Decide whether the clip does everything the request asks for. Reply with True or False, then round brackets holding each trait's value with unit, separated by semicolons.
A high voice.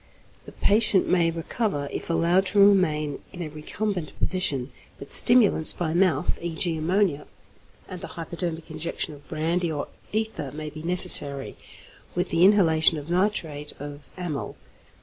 False (165 Hz)